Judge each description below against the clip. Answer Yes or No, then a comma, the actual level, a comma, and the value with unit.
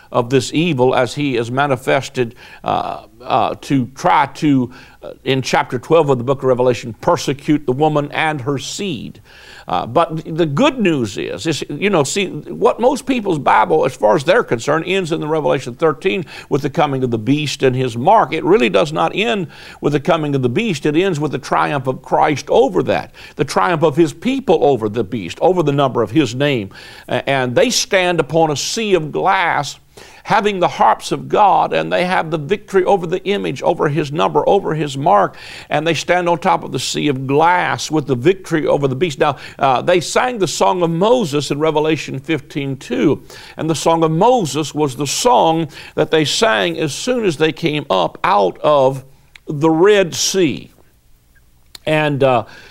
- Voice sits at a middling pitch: Yes, medium, 155 Hz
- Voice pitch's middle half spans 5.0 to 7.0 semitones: No, average, 4.4 semitones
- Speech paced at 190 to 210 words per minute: Yes, average, 195 wpm